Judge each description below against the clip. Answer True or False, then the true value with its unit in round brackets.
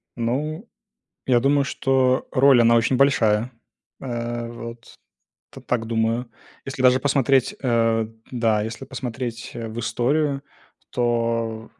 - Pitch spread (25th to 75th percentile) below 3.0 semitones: True (2.5 semitones)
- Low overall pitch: True (120 Hz)